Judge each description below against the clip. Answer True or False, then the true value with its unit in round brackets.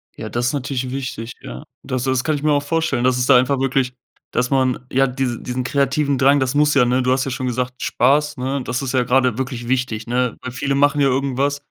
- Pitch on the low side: True (130 Hz)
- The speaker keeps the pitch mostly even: True (1.8 semitones)